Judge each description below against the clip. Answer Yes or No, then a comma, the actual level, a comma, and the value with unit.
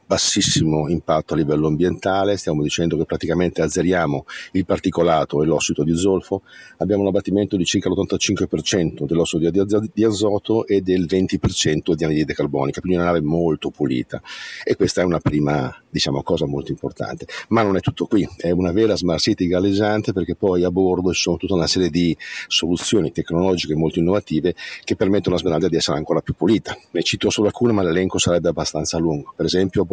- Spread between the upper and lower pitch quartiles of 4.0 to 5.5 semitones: No, average, 3.0 semitones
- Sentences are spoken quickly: Yes, fast, 180 wpm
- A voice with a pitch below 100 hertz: Yes, very low, 90 Hz